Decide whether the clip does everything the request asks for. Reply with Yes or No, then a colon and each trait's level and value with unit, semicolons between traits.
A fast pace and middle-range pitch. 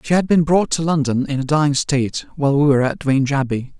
Yes: fast, 255 wpm; medium, 145 Hz